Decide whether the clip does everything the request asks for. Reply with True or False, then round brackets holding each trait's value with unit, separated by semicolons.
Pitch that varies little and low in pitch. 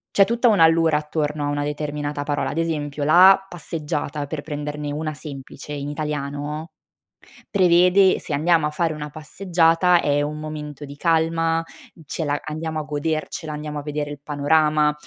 False (1.9 semitones; 150 Hz)